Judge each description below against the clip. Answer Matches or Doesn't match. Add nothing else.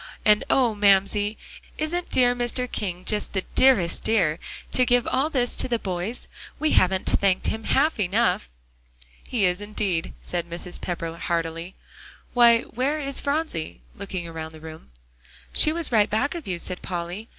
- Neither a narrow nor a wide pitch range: Doesn't match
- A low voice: Doesn't match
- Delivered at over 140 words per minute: Matches